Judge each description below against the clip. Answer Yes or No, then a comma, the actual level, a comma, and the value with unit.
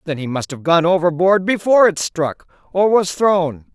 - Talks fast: No, average, 175 wpm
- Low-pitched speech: No, medium, 180 Hz